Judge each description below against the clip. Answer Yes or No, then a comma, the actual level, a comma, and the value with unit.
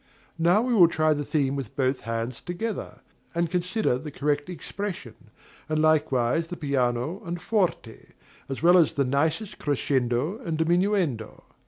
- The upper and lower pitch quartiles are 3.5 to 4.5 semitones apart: No, average, 4.9 semitones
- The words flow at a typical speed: Yes, average, 150 wpm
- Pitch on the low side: No, medium, 155 Hz